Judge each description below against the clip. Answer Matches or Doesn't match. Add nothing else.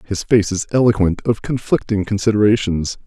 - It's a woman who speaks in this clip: Doesn't match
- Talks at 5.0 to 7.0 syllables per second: Matches